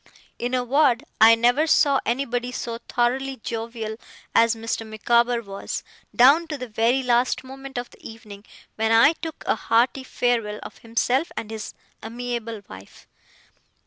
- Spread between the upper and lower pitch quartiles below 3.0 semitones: Yes, narrow, 2.4 semitones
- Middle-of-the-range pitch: No, high, 240 Hz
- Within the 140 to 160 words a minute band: Yes, average, 150 wpm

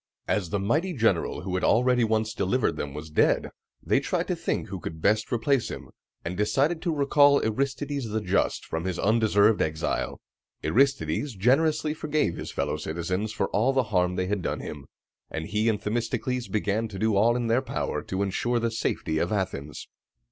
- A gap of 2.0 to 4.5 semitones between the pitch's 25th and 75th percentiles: No, average, 5.2 semitones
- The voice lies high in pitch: No, low, 110 Hz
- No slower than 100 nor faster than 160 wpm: No, average, 185 wpm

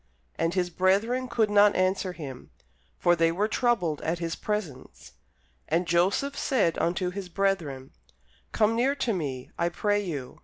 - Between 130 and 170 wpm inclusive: Yes, average, 155 wpm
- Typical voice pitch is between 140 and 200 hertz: Yes, medium, 185 Hz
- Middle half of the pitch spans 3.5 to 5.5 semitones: Yes, average, 4.0 semitones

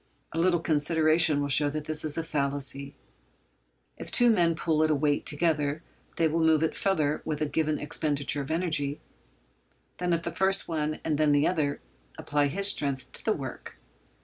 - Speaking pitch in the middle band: Yes, medium, 155 Hz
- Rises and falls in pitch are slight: Yes, narrow, 2.2 semitones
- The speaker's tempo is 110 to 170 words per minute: No, average, 180 wpm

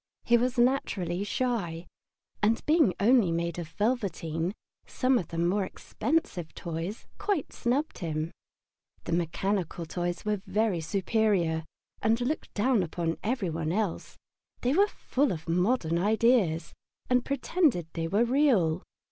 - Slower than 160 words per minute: Yes, slow, 135 wpm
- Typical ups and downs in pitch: No, wide, 6.4 semitones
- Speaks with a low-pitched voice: No, high, 200 Hz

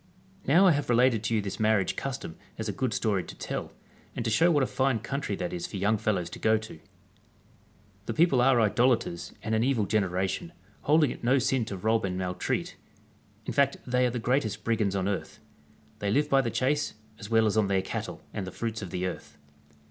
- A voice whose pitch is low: Yes, low, 110 Hz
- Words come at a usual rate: No, fast, 220 wpm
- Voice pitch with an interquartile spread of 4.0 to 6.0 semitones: Yes, average, 4.7 semitones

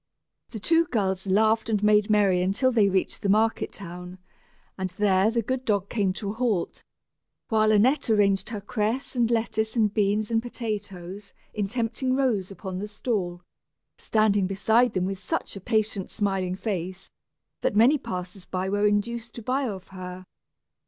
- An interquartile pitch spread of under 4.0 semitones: Yes, average, 2.8 semitones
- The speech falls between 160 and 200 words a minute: Yes, average, 165 wpm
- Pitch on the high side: Yes, high, 210 Hz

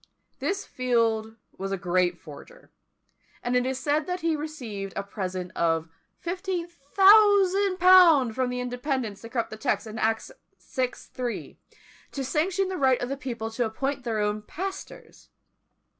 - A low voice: No, very high, 255 Hz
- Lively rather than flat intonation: Yes, wide, 7.6 semitones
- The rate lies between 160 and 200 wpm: No, average, 150 wpm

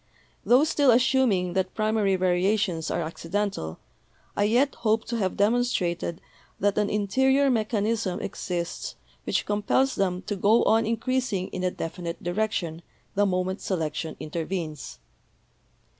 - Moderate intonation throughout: Yes, average, 4.0 semitones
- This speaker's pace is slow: Yes, slow, 130 wpm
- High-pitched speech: Yes, high, 200 Hz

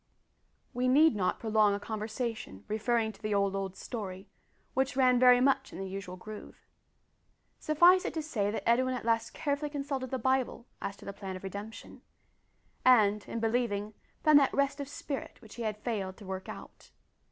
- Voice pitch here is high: Yes, high, 225 Hz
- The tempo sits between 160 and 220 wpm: Yes, average, 185 wpm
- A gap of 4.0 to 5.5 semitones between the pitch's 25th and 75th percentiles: Yes, average, 4.4 semitones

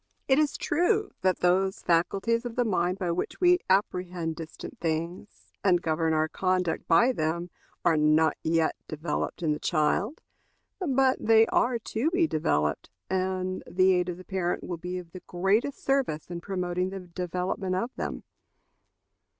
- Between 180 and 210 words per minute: No, average, 160 wpm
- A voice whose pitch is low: No, medium, 180 Hz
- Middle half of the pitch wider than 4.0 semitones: Yes, average, 4.5 semitones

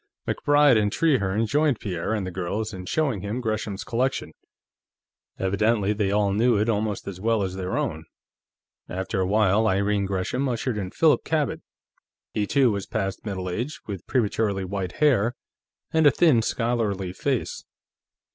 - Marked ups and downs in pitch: No, average, 3.7 semitones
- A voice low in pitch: Yes, low, 105 Hz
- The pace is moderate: Yes, average, 155 wpm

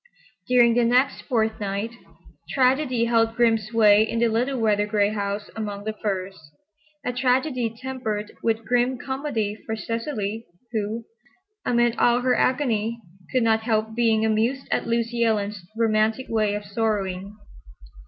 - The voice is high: Yes, high, 225 Hz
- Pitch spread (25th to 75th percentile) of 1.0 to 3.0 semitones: Yes, narrow, 2.5 semitones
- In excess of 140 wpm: No, slow, 135 wpm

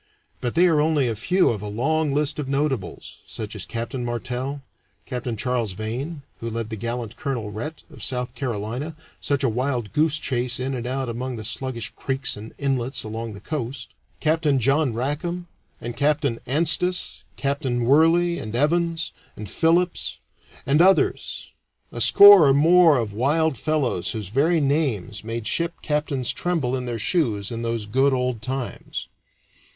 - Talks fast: No, average, 165 wpm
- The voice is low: Yes, low, 130 Hz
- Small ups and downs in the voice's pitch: No, average, 4.6 semitones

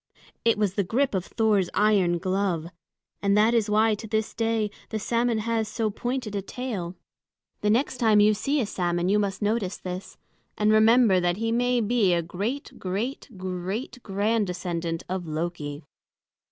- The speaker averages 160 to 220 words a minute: Yes, average, 170 wpm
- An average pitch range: Yes, average, 3.7 semitones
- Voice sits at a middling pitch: No, high, 210 Hz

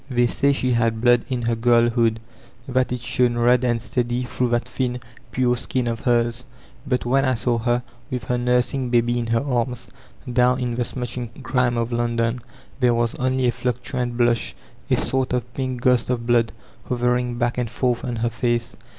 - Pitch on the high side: No, low, 120 Hz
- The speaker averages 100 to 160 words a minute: No, average, 190 wpm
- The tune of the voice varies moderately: No, narrow, 1.1 semitones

